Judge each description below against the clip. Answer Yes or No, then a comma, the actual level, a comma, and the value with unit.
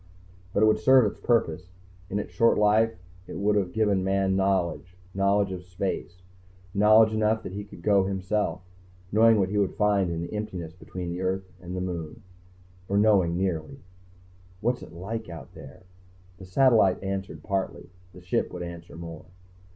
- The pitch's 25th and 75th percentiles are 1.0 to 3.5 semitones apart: Yes, average, 2.7 semitones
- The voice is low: Yes, very low, 95 Hz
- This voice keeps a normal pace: Yes, average, 175 wpm